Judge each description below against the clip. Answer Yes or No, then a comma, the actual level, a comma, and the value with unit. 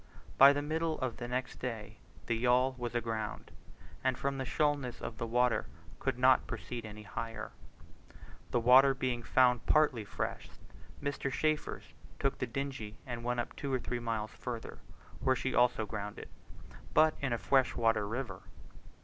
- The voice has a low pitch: Yes, low, 125 Hz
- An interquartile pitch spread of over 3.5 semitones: No, average, 2.7 semitones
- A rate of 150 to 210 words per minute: Yes, average, 165 wpm